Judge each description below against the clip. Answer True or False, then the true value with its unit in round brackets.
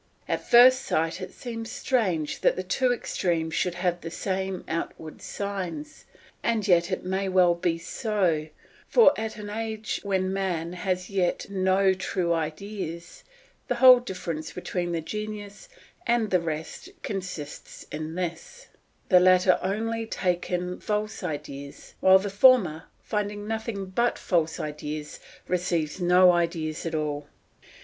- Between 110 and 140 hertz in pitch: False (185 Hz)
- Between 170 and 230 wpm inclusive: False (145 wpm)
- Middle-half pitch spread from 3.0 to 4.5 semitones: True (3.8 semitones)